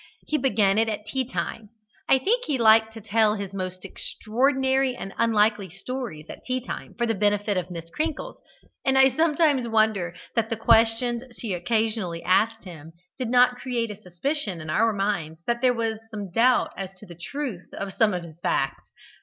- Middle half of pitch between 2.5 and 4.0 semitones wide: No, average, 4.4 semitones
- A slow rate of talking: No, average, 185 wpm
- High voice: Yes, high, 220 Hz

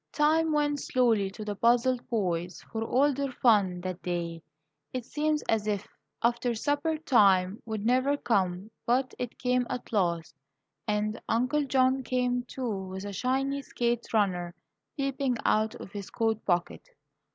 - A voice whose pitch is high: Yes, high, 235 Hz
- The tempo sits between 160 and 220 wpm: No, average, 150 wpm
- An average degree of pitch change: Yes, average, 4.6 semitones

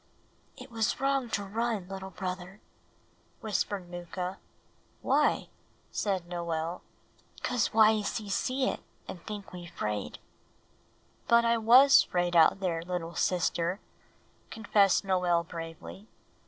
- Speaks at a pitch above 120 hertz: Yes, high, 190 Hz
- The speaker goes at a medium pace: No, slow, 115 wpm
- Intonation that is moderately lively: Yes, average, 4.0 semitones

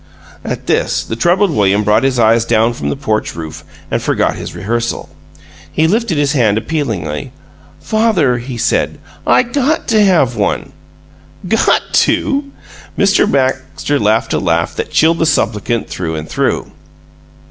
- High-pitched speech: No, low, 125 Hz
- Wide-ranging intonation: Yes, wide, 7.9 semitones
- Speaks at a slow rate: No, average, 150 wpm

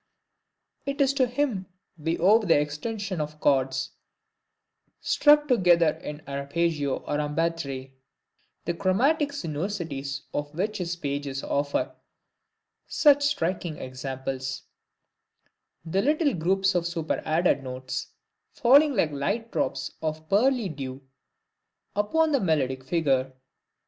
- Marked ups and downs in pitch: Yes, wide, 7.0 semitones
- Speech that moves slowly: Yes, slow, 115 wpm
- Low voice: No, medium, 165 Hz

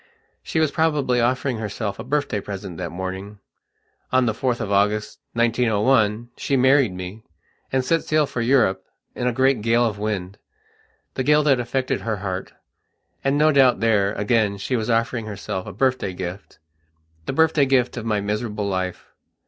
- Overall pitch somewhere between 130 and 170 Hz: No, low, 115 Hz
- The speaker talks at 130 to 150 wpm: No, average, 165 wpm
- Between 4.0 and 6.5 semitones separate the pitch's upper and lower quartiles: Yes, average, 4.3 semitones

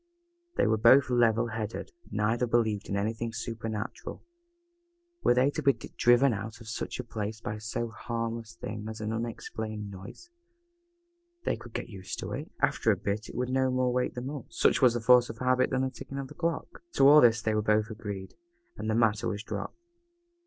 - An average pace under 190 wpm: No, average, 200 wpm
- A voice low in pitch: Yes, low, 115 Hz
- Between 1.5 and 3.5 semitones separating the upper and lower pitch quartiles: Yes, narrow, 2.5 semitones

